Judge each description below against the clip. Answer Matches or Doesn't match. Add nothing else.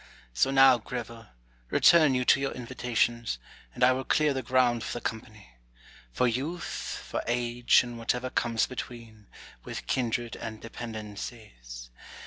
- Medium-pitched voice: Doesn't match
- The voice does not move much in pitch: Matches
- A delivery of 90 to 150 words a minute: Matches